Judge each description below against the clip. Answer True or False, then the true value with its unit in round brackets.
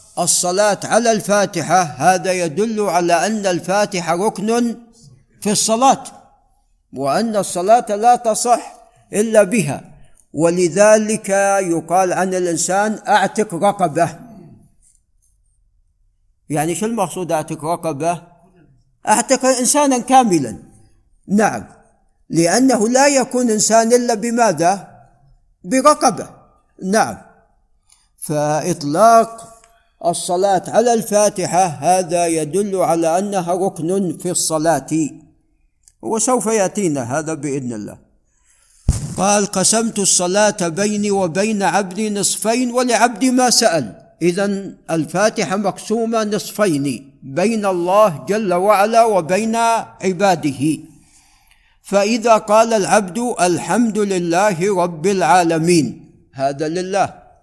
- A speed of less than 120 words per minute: True (90 wpm)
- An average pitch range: True (4.4 semitones)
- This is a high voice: True (195 Hz)